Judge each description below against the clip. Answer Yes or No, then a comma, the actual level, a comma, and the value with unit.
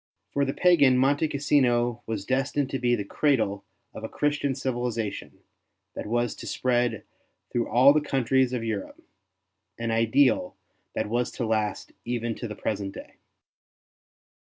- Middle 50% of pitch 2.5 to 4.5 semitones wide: Yes, average, 3.0 semitones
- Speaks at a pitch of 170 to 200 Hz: No, low, 120 Hz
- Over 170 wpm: No, average, 155 wpm